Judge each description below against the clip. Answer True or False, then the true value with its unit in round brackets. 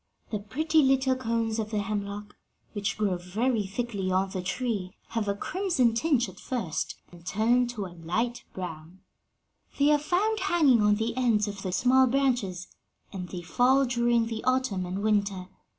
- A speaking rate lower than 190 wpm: True (170 wpm)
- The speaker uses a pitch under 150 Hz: False (220 Hz)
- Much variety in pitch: False (4.6 semitones)